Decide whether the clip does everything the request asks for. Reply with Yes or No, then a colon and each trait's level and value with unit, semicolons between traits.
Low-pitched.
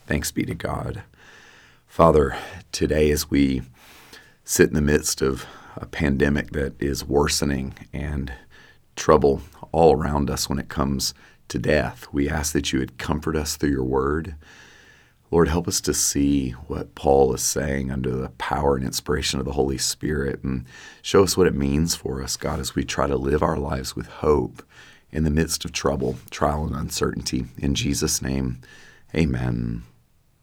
Yes: very low, 70 Hz